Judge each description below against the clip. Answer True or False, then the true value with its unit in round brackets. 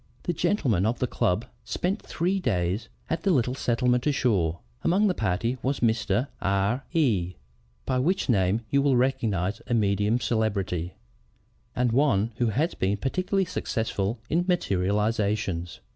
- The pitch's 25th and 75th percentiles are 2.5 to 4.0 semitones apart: False (5.4 semitones)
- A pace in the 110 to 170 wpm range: True (145 wpm)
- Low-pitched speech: True (115 Hz)